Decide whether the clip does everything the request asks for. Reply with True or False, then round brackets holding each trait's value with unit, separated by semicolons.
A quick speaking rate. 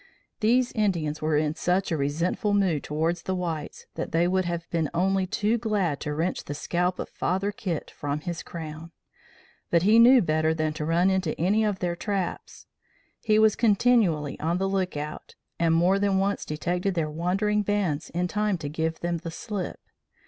False (185 wpm)